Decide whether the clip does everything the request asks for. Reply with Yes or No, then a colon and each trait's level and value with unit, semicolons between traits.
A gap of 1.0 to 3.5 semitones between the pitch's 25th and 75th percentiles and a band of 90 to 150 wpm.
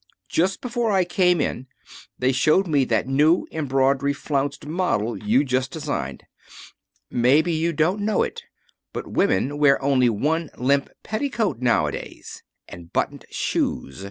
No: average, 5.0 semitones; slow, 135 wpm